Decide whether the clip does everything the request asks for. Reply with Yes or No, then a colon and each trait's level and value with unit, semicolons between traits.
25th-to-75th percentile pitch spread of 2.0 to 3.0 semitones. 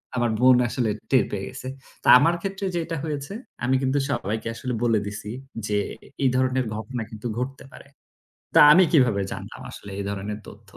No: average, 4.0 semitones